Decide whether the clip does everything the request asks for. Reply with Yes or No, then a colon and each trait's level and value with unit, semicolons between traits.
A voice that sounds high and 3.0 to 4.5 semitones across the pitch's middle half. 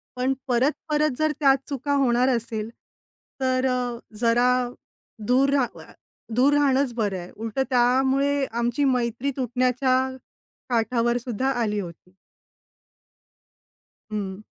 No: very high, 250 Hz; narrow, 2.6 semitones